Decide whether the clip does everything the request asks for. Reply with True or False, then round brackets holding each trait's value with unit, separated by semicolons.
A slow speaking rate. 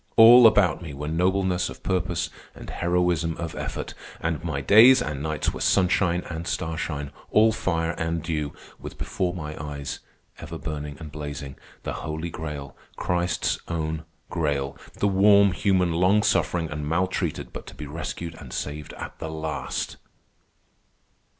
False (150 wpm)